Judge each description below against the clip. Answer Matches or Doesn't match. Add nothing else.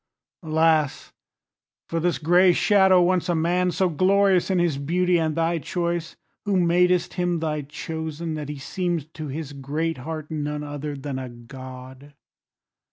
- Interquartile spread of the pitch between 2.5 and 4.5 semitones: Matches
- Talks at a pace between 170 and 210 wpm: Doesn't match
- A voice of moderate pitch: Matches